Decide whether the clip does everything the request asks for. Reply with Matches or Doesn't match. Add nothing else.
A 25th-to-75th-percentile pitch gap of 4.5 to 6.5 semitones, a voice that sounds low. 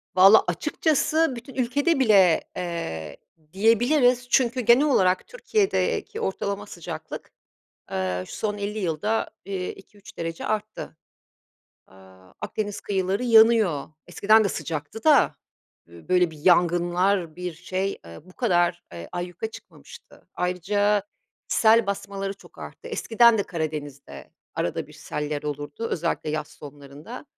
Doesn't match